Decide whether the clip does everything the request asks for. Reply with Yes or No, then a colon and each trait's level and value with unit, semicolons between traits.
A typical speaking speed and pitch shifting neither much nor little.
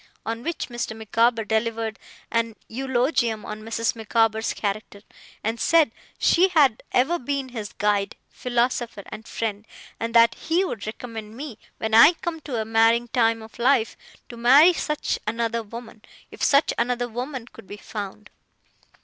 No: average, 155 wpm; narrow, 2.3 semitones